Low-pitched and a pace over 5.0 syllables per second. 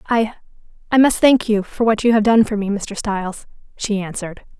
No: high, 215 Hz; 5.5 syllables/s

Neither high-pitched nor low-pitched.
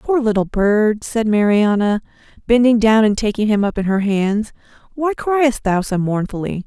No: high, 220 Hz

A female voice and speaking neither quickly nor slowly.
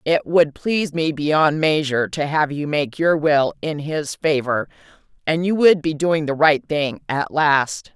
Yes: female; average, 190 wpm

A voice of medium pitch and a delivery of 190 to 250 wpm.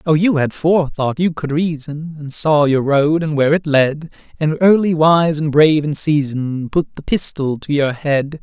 Yes: medium, 150 Hz; average, 200 wpm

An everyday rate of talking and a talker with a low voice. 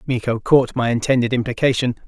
Yes: average, 145 wpm; low, 120 Hz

